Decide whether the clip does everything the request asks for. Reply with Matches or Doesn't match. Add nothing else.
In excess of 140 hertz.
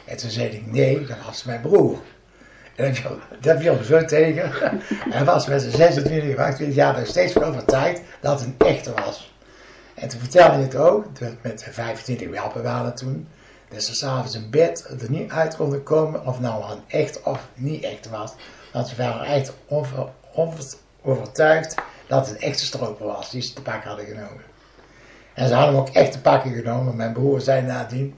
Doesn't match